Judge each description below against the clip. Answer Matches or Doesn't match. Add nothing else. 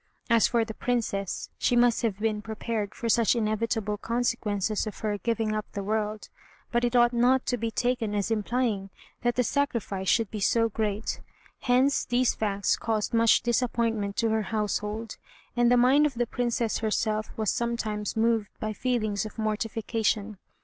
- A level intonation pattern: Matches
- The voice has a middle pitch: Doesn't match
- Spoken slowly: Doesn't match